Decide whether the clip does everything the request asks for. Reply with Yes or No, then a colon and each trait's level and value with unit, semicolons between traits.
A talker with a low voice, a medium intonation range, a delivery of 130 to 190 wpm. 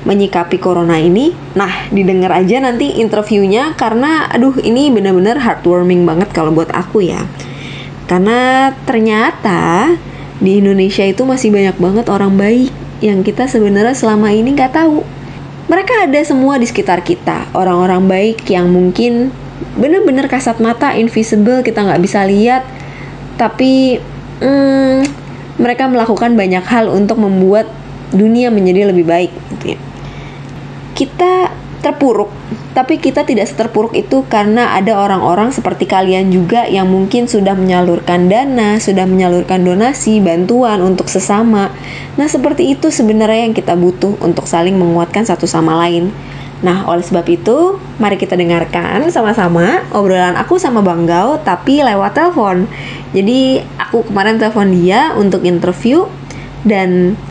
No: high, 205 Hz; average, 5.0 semitones; average, 135 wpm